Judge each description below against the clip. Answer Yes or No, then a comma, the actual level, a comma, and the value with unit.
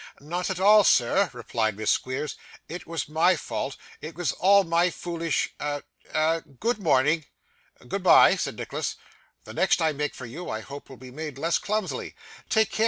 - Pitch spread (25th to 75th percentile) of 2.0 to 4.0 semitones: No, average, 4.4 semitones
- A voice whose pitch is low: No, medium, 160 Hz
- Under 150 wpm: No, average, 175 wpm